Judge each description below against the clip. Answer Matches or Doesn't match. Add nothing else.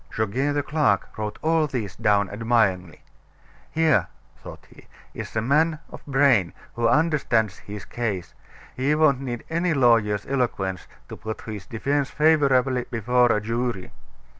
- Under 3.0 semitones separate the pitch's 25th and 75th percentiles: Doesn't match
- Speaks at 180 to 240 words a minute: Doesn't match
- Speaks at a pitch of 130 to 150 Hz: Doesn't match